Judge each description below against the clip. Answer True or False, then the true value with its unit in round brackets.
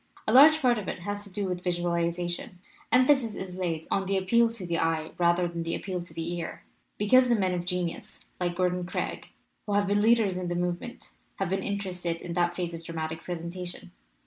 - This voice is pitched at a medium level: True (180 Hz)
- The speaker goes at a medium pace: False (210 wpm)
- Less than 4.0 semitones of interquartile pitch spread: True (2.8 semitones)